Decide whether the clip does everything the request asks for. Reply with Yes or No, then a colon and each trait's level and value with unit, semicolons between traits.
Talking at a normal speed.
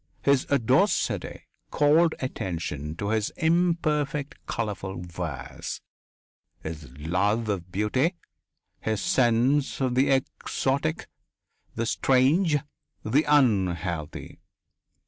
No: slow, 90 wpm